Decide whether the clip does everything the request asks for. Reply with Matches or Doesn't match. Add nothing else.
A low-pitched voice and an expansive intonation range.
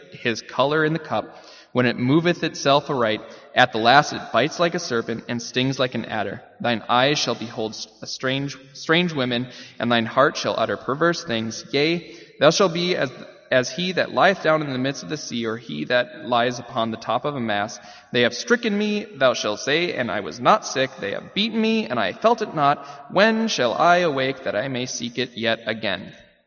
Matches